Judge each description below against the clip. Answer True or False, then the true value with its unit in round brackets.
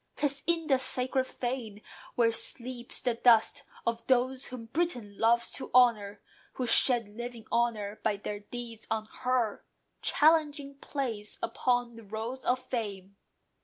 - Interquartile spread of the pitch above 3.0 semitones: False (2.7 semitones)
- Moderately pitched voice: False (240 Hz)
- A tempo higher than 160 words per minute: False (140 wpm)